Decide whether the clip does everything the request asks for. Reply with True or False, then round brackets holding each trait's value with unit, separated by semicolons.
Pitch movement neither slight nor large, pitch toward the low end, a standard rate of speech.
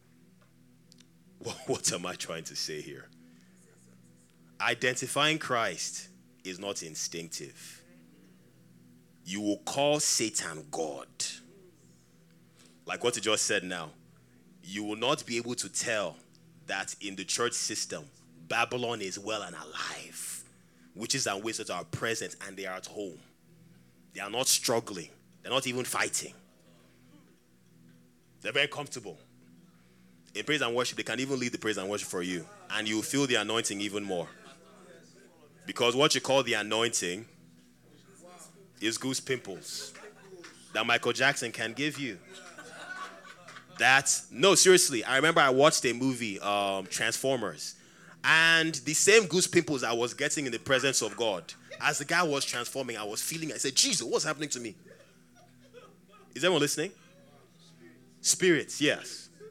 False (8.2 semitones; 110 Hz; 145 wpm)